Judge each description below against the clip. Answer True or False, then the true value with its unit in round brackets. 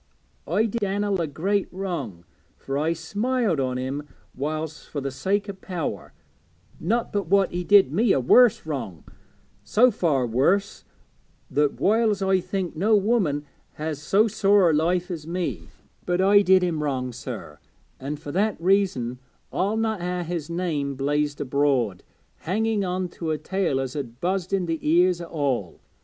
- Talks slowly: False (170 wpm)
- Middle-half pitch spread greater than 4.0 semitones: True (5.4 semitones)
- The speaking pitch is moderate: True (170 Hz)